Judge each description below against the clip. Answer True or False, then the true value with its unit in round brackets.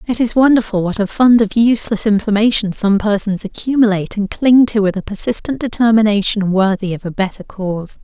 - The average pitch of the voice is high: True (210 Hz)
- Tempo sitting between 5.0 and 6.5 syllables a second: True (5.7 syllables/s)